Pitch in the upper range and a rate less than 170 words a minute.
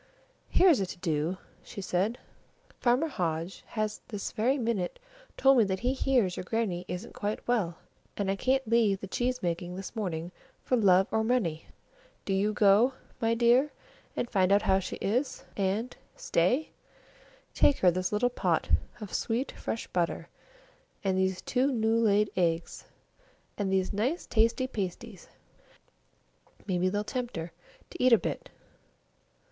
Yes: high, 210 Hz; average, 155 wpm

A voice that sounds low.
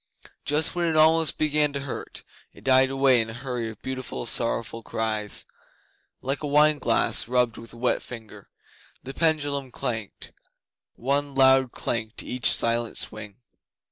Yes: low, 130 Hz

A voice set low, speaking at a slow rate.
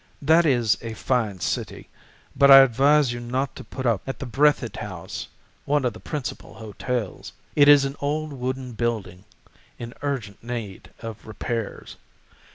No: low, 125 Hz; average, 160 wpm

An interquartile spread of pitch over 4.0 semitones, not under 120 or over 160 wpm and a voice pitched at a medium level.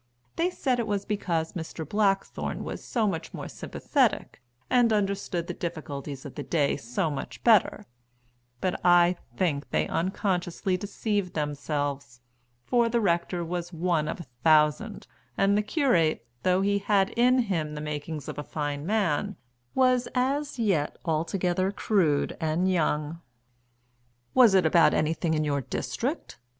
Yes: average, 5.0 semitones; average, 145 wpm; medium, 175 Hz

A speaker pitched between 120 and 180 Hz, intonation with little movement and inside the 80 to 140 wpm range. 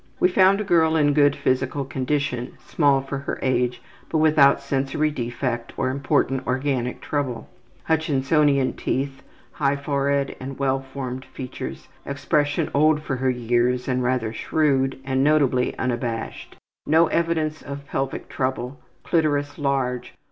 Yes: medium, 140 Hz; narrow, 2.2 semitones; slow, 135 wpm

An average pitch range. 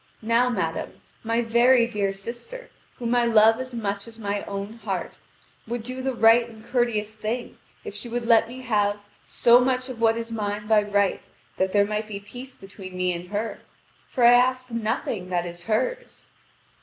Yes: average, 3.0 semitones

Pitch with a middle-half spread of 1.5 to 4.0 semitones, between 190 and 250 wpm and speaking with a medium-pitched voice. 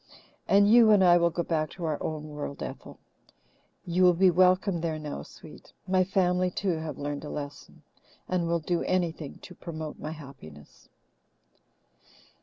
No: average, 3.0 semitones; average, 165 wpm; medium, 170 Hz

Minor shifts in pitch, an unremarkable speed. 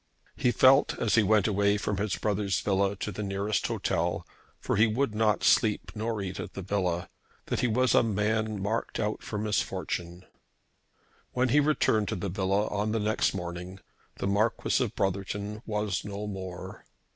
Yes: narrow, 2.0 semitones; average, 175 wpm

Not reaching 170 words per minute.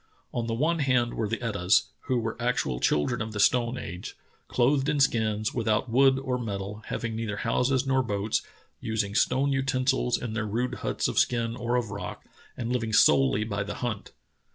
No: average, 190 wpm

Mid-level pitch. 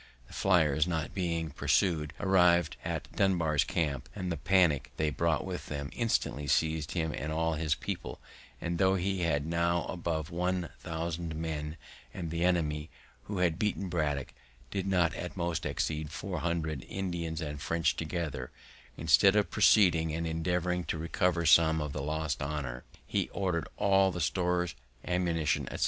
No: very low, 85 Hz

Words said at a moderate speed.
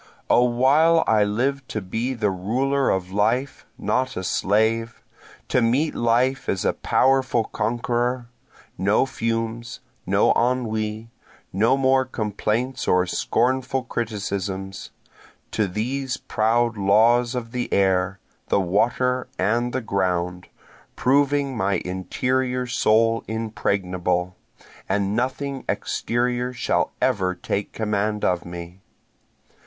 No: slow, 115 wpm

